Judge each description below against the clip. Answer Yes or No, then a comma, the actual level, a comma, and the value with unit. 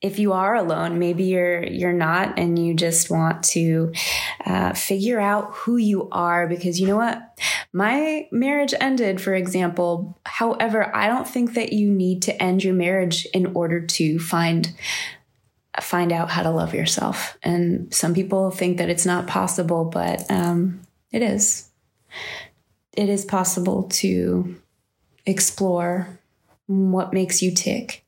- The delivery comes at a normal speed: Yes, average, 150 wpm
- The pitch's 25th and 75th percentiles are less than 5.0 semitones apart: Yes, narrow, 2.5 semitones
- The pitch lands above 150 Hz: Yes, medium, 185 Hz